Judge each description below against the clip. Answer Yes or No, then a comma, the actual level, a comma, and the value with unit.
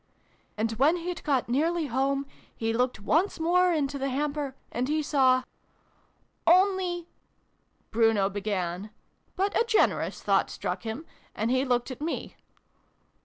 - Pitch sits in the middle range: No, very high, 275 Hz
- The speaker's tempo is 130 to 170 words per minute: Yes, average, 150 wpm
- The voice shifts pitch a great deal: Yes, wide, 5.9 semitones